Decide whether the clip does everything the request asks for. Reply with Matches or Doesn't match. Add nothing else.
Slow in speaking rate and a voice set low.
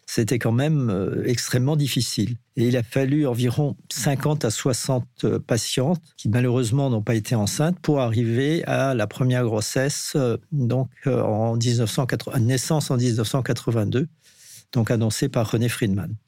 Matches